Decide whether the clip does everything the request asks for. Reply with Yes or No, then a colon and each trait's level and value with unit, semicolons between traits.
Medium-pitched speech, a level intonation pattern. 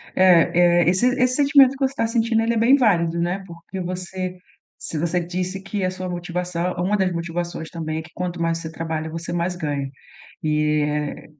Yes: medium, 175 Hz; narrow, 2.3 semitones